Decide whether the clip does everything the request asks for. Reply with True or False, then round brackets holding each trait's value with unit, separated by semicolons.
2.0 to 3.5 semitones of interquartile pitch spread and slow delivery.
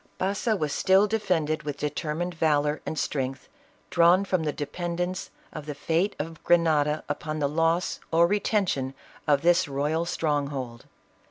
False (3.0 semitones; 150 wpm)